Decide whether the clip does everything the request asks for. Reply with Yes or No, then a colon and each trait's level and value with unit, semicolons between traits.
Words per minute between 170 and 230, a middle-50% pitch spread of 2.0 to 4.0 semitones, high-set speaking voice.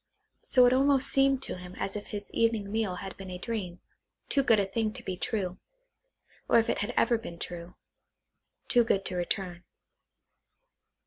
No: average, 180 wpm; average, 4.4 semitones; high, 205 Hz